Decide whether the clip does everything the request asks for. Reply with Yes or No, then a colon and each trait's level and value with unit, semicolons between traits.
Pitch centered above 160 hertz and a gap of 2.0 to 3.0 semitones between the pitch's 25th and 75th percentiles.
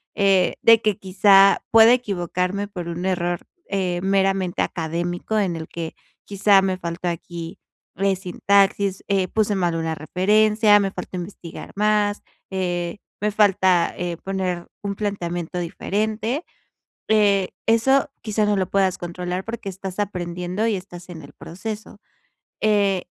Yes: high, 190 Hz; average, 2.7 semitones